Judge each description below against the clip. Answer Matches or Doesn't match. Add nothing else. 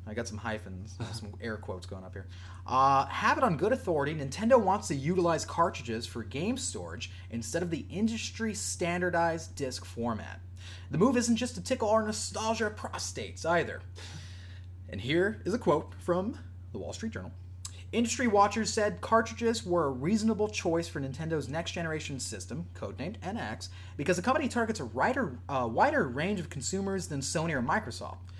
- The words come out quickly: Doesn't match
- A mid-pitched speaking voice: Doesn't match